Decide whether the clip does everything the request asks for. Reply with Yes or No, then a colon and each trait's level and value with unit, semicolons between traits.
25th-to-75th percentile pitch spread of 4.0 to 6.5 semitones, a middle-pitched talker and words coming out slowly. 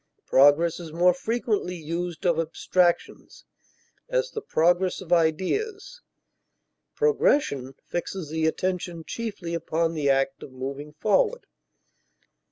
Yes: average, 4.9 semitones; medium, 175 Hz; slow, 110 wpm